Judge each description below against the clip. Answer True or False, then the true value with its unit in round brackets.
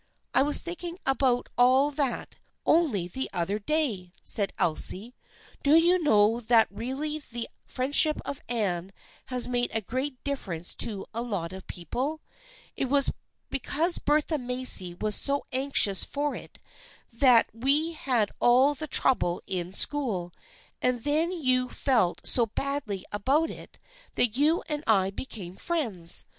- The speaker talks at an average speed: True (150 wpm)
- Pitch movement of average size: False (5.8 semitones)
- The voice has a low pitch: False (250 Hz)